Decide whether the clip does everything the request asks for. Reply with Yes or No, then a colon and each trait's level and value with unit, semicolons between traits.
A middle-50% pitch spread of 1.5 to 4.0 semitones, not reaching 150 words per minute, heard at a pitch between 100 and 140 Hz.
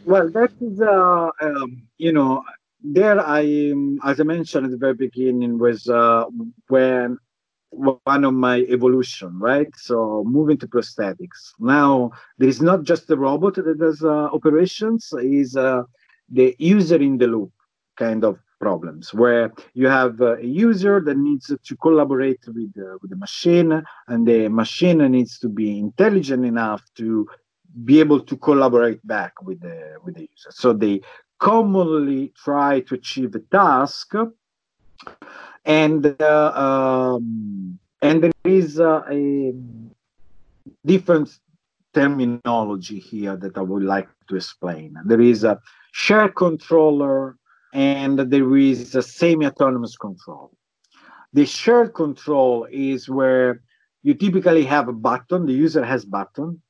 No: average, 5.1 semitones; average, 140 wpm; low, 135 Hz